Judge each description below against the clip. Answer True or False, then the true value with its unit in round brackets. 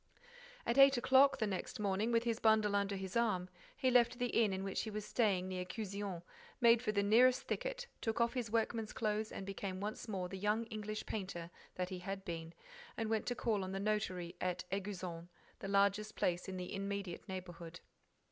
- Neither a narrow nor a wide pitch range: True (3.2 semitones)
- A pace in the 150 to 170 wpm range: False (195 wpm)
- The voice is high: True (205 Hz)